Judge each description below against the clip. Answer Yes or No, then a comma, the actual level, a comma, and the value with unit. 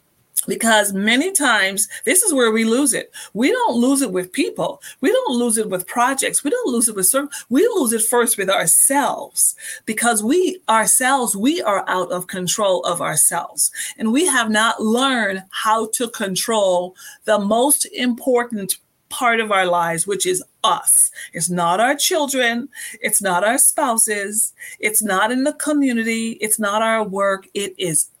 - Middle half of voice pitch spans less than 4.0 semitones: No, wide, 5.4 semitones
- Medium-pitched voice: No, high, 225 Hz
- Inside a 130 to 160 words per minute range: No, average, 170 wpm